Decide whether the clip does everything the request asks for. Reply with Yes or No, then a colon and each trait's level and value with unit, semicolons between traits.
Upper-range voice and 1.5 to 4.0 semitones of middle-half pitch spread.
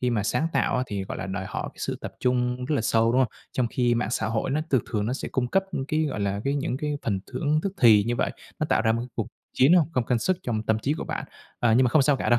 No: low, 125 Hz; average, 3.3 semitones